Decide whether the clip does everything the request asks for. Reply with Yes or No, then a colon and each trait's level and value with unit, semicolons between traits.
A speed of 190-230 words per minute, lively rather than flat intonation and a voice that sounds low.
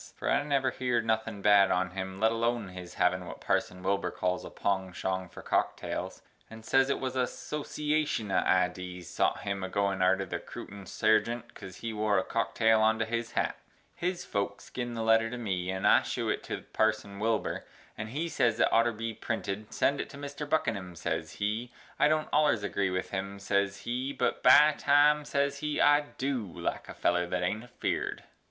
No: average, 195 wpm; average, 4.7 semitones; low, 110 Hz